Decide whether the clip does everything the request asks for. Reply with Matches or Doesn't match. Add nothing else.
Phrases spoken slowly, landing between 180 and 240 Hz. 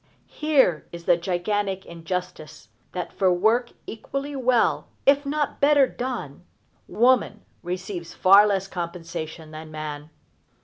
Matches